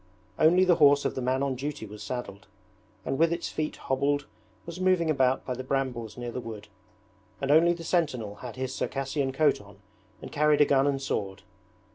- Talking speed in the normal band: Yes, average, 195 wpm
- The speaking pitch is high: No, low, 135 Hz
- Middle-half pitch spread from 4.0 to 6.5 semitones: No, average, 3.6 semitones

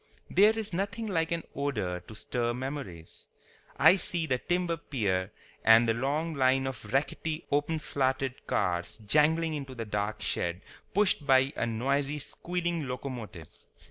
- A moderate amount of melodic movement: No, wide, 6.0 semitones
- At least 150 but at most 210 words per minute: No, average, 140 wpm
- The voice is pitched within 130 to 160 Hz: Yes, low, 135 Hz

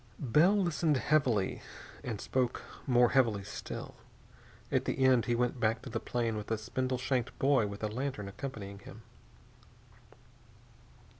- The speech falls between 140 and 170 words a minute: Yes, average, 145 wpm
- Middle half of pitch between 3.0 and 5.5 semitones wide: Yes, average, 3.5 semitones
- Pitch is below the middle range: Yes, low, 125 Hz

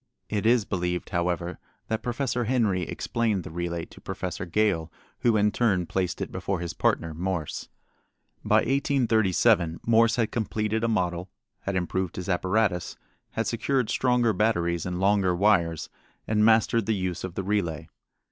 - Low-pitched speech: Yes, low, 100 Hz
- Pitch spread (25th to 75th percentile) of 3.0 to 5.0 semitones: Yes, average, 4.2 semitones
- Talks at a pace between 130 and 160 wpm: Yes, average, 155 wpm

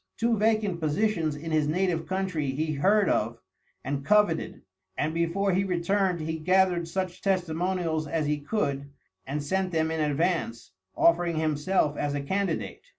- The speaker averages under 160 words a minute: Yes, average, 150 wpm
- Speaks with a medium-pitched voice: Yes, medium, 165 Hz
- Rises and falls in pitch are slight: No, average, 3.9 semitones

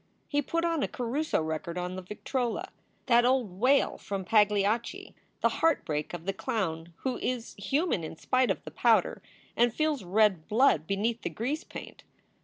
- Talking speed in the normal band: Yes, average, 165 wpm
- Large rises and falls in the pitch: Yes, wide, 5.9 semitones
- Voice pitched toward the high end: Yes, high, 225 Hz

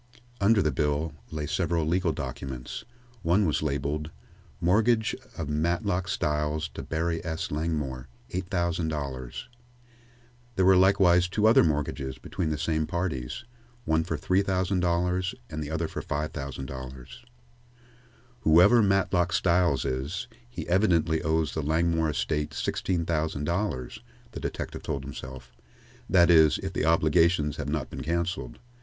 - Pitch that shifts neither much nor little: Yes, average, 3.2 semitones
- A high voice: No, very low, 80 Hz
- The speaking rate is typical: No, slow, 130 wpm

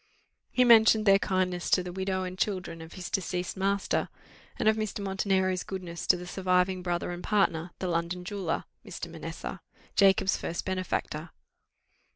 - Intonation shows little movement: Yes, narrow, 1.6 semitones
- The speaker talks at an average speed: Yes, average, 160 wpm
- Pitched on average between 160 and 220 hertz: Yes, medium, 185 Hz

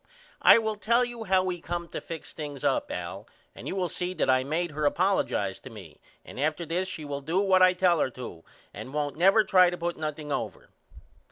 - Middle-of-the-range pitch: Yes, medium, 170 Hz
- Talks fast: Yes, fast, 225 wpm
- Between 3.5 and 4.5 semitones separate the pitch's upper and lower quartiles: Yes, average, 4.2 semitones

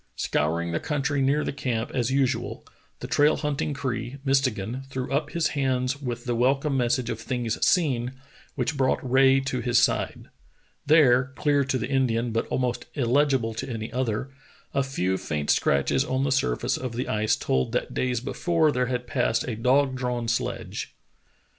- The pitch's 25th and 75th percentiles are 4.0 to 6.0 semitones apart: No, average, 2.8 semitones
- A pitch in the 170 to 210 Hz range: No, low, 125 Hz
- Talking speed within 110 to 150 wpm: No, average, 170 wpm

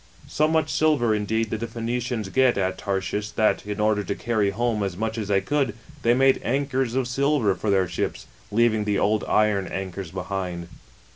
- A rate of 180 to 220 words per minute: Yes, average, 195 wpm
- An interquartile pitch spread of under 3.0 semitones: No, average, 3.5 semitones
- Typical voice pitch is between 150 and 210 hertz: No, low, 110 Hz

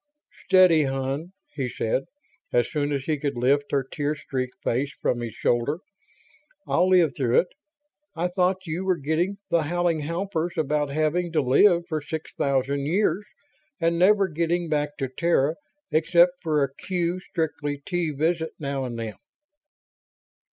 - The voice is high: No, medium, 155 Hz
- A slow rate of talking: No, average, 155 wpm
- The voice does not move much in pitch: No, average, 3.9 semitones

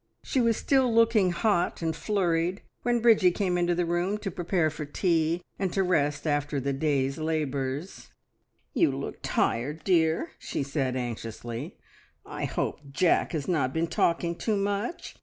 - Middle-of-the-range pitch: Yes, medium, 170 Hz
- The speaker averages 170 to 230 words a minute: No, average, 160 wpm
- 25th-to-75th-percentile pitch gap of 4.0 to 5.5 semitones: Yes, average, 4.9 semitones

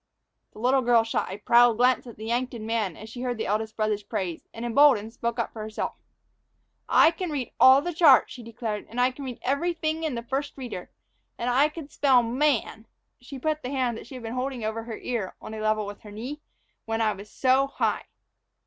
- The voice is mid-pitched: No, high, 240 Hz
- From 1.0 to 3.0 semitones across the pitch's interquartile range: No, average, 3.5 semitones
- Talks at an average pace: No, fast, 220 wpm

